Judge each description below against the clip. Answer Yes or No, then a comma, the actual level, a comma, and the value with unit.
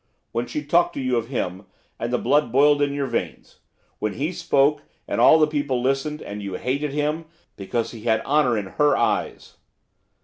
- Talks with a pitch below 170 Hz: Yes, low, 135 Hz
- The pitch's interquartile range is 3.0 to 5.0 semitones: Yes, average, 4.1 semitones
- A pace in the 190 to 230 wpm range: Yes, average, 195 wpm